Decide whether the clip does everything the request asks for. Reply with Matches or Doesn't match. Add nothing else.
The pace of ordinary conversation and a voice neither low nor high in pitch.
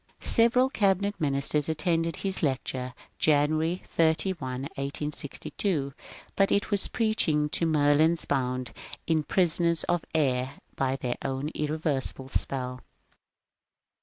Doesn't match